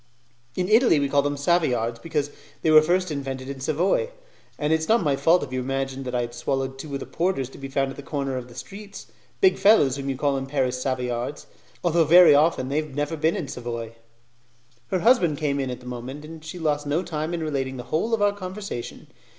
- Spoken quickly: Yes, fast, 230 wpm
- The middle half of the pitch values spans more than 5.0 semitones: No, average, 3.8 semitones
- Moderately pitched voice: Yes, medium, 145 Hz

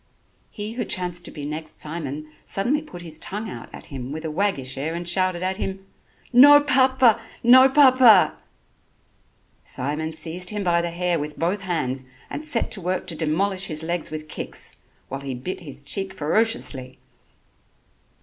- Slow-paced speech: No, average, 170 wpm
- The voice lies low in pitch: No, medium, 175 Hz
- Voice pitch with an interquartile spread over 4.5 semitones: Yes, average, 5.1 semitones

